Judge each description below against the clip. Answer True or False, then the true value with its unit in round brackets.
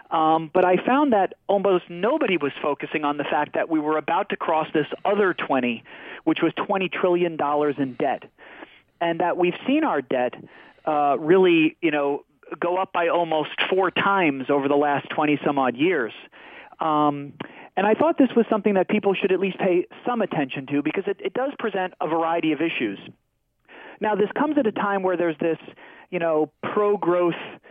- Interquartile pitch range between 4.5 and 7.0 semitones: True (4.8 semitones)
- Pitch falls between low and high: True (175 Hz)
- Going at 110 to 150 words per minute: False (190 wpm)